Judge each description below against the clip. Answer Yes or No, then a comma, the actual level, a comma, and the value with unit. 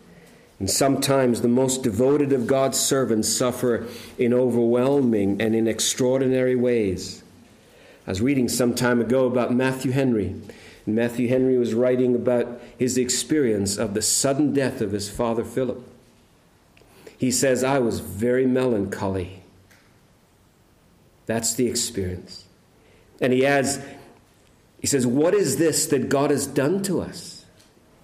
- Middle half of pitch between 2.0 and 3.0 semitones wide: Yes, narrow, 2.5 semitones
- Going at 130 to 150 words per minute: Yes, slow, 135 wpm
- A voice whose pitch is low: Yes, low, 125 Hz